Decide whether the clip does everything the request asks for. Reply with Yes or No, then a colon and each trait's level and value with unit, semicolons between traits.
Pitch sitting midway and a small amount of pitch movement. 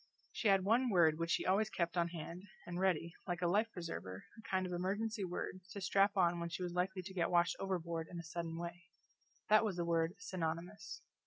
Yes: medium, 180 Hz; narrow, 2.3 semitones